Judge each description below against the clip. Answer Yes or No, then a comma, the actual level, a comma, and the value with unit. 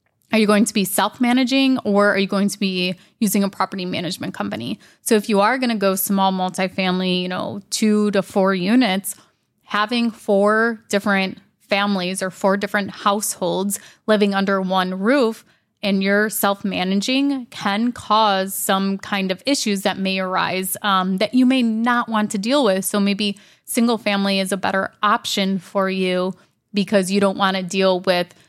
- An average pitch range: No, narrow, 2.0 semitones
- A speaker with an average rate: Yes, average, 175 wpm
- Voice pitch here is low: No, high, 200 Hz